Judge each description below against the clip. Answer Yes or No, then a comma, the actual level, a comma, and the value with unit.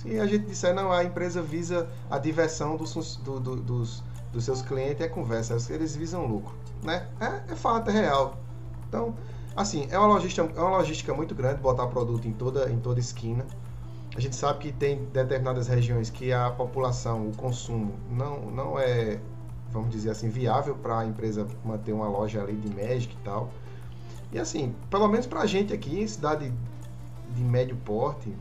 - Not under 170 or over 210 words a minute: Yes, average, 180 wpm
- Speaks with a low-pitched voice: Yes, low, 125 Hz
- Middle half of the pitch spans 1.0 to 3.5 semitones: Yes, average, 3.2 semitones